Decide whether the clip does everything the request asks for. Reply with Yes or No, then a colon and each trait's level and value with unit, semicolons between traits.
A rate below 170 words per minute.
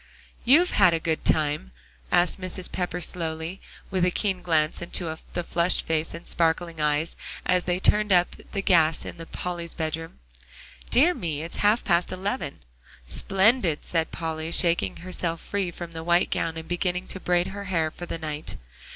No: average, 175 wpm